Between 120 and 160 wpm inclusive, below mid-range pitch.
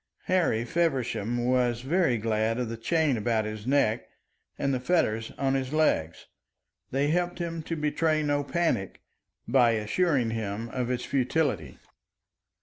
Yes: average, 145 wpm; low, 125 Hz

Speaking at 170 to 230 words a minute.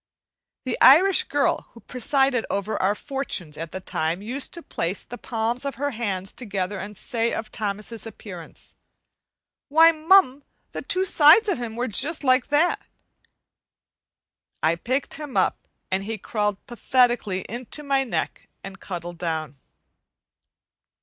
No: average, 145 wpm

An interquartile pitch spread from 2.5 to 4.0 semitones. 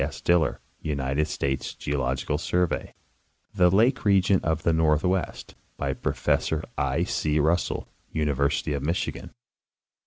Yes: average, 3.6 semitones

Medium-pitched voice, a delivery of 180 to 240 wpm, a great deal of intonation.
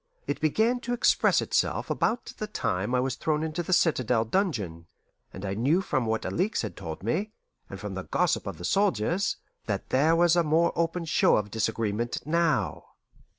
Yes: medium, 155 Hz; average, 185 wpm; wide, 7.8 semitones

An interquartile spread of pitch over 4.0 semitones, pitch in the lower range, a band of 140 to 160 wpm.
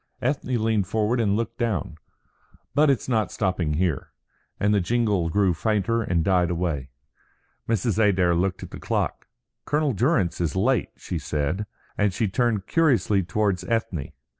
Yes: average, 4.5 semitones; low, 105 Hz; average, 155 wpm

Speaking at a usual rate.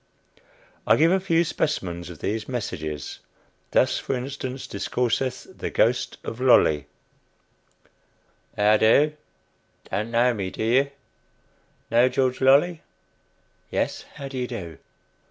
No: slow, 120 wpm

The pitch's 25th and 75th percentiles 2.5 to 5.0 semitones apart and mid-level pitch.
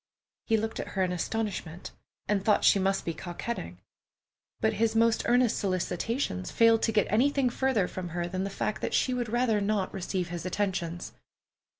No: average, 3.9 semitones; high, 205 Hz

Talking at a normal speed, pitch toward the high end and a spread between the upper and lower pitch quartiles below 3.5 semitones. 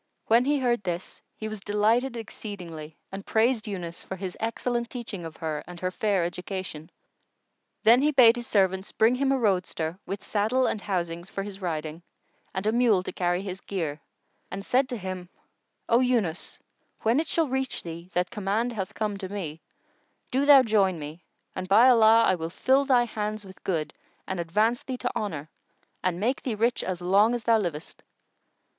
No: average, 185 wpm; high, 205 Hz; average, 4.8 semitones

